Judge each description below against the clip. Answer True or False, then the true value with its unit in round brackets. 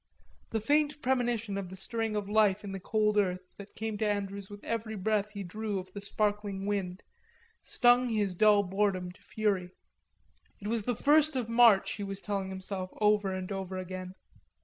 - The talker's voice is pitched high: True (205 Hz)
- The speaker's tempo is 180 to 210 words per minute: True (185 wpm)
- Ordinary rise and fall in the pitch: False (2.3 semitones)